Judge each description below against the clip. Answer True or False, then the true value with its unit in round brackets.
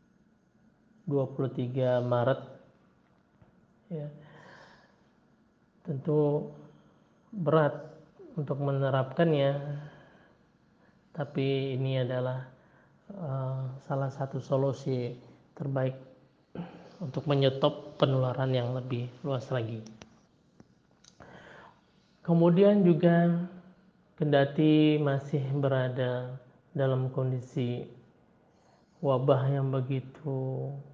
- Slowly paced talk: True (60 wpm)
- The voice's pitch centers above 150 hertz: False (140 Hz)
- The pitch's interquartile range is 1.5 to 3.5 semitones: True (2.8 semitones)